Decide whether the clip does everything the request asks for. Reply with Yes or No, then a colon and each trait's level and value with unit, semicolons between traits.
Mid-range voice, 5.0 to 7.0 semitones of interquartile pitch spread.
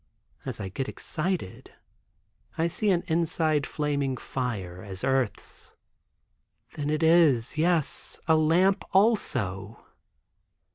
Yes: medium, 150 Hz; average, 5.3 semitones